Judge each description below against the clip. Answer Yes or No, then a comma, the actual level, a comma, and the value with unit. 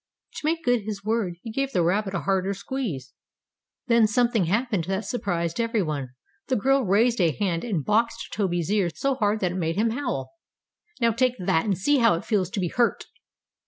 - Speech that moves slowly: No, average, 200 wpm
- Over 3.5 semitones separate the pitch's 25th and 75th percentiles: Yes, average, 4.6 semitones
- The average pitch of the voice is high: Yes, high, 210 Hz